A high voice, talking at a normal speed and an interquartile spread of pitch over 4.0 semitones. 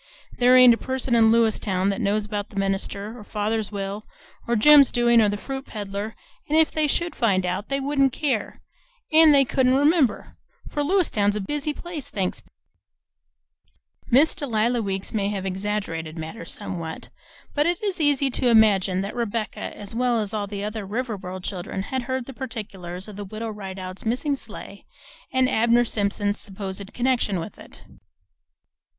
Yes: high, 220 Hz; average, 170 wpm; average, 4.6 semitones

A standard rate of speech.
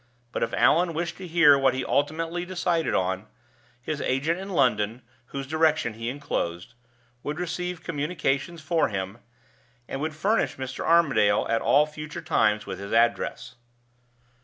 Yes: average, 150 wpm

